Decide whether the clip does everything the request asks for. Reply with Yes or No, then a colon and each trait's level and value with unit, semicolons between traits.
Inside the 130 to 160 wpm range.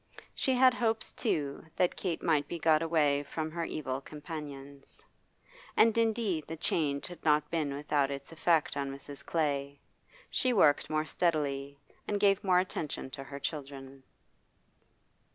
Yes: average, 150 wpm